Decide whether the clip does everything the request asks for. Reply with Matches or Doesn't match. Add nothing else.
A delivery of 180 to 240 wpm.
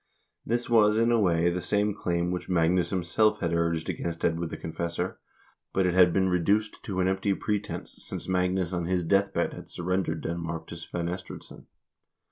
Matches